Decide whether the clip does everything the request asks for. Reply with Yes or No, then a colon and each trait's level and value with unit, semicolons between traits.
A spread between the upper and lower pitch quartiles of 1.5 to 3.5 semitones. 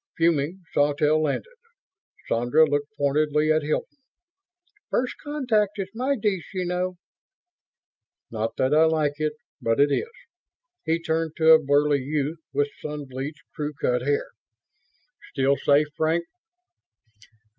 Yes: average, 2.8 semitones